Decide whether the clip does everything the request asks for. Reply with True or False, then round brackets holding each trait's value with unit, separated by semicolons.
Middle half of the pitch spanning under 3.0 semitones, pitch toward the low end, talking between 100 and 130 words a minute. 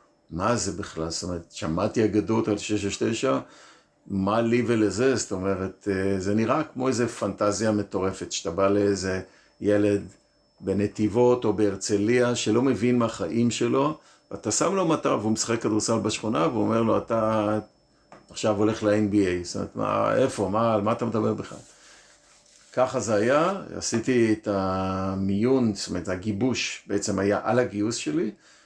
False (2.6 semitones; 105 Hz; 150 wpm)